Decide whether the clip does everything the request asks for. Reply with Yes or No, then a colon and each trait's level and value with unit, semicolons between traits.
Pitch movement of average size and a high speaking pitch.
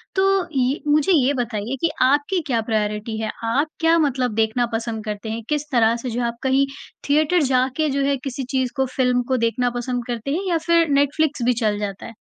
Yes: average, 4.0 semitones; very high, 255 Hz